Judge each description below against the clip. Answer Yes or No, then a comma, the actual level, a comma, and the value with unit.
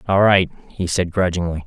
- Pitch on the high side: No, very low, 90 Hz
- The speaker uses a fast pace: No, average, 180 wpm